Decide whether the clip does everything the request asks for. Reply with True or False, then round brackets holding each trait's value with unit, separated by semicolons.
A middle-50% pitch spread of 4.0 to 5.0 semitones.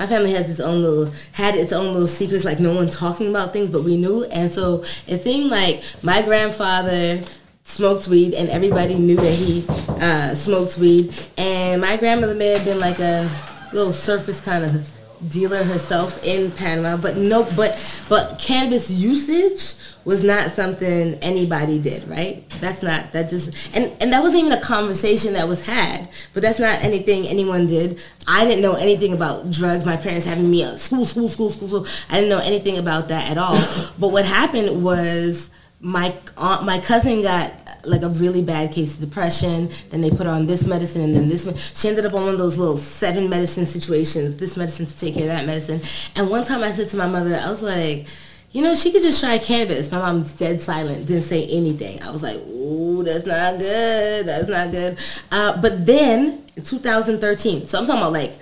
False (3.4 semitones)